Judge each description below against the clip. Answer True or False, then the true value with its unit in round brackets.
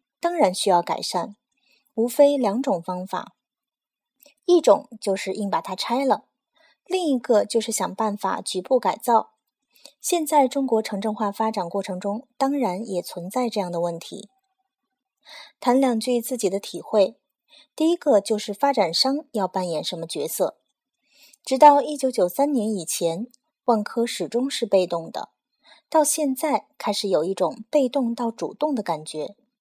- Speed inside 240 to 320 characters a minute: False (225 characters per minute)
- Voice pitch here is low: False (240 Hz)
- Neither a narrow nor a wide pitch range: False (6.0 semitones)